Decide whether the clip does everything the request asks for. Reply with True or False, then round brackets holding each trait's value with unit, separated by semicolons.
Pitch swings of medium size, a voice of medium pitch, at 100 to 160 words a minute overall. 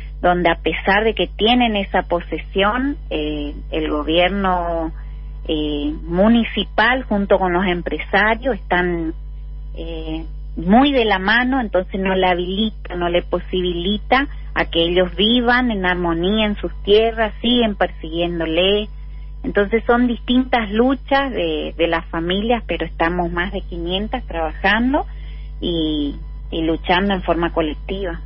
True (4.4 semitones; 180 Hz; 130 wpm)